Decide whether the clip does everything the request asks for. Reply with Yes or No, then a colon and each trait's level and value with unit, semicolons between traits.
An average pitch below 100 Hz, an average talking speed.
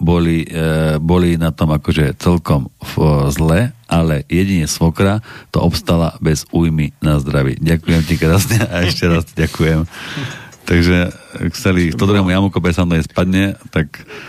Yes: very low, 85 Hz; average, 125 wpm